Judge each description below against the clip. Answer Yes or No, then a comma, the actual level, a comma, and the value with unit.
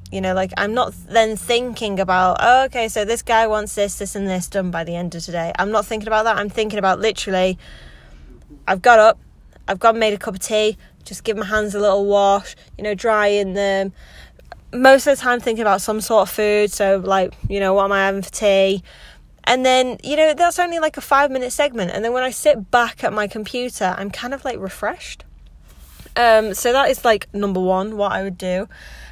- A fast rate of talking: Yes, fast, 225 wpm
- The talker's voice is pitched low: No, high, 210 Hz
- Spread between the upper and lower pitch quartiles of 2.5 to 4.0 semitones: Yes, average, 3.6 semitones